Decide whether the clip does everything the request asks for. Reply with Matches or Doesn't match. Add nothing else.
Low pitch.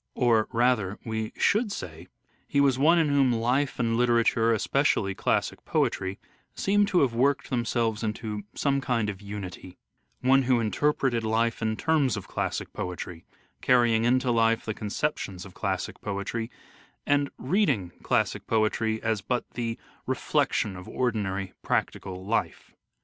Matches